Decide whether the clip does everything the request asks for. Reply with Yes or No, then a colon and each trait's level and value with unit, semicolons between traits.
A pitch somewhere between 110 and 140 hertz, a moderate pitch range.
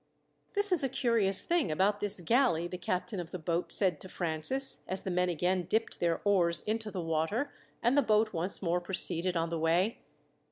No: medium, 185 Hz; average, 4.4 semitones